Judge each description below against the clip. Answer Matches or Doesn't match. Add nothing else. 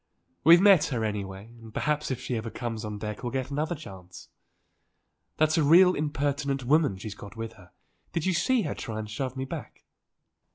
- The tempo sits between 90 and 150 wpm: Doesn't match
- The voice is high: Doesn't match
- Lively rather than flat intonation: Matches